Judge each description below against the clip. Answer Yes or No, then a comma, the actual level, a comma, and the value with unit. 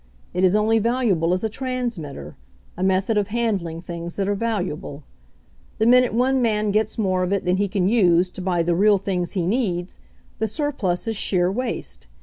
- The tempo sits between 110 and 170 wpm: No, average, 190 wpm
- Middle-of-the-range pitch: No, high, 195 Hz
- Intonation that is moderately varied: Yes, average, 3.9 semitones